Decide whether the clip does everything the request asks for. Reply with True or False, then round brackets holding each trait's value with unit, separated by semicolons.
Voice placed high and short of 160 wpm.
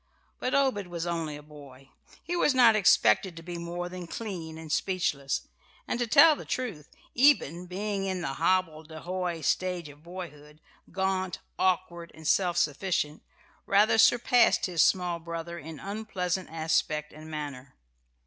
False (175 Hz; 150 wpm)